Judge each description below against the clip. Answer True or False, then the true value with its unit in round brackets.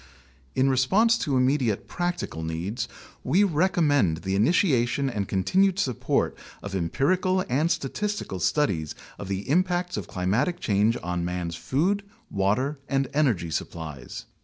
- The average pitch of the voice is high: False (130 Hz)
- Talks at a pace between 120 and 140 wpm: True (135 wpm)